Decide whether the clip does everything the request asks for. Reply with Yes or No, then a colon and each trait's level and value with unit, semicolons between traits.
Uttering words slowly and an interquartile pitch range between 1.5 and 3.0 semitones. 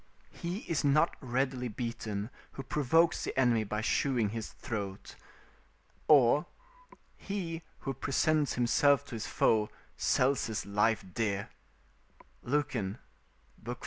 No: slow, 115 wpm; average, 4.6 semitones